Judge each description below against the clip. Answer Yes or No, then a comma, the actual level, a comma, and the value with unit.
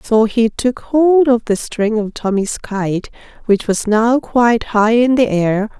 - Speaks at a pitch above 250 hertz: No, high, 225 Hz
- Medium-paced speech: Yes, average, 185 wpm